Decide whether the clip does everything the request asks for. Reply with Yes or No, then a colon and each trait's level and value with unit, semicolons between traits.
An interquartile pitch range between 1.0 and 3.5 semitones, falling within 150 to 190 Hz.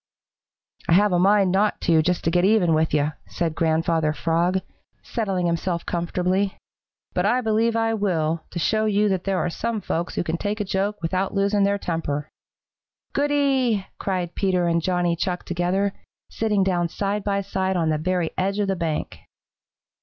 Yes: average, 3.2 semitones; medium, 185 Hz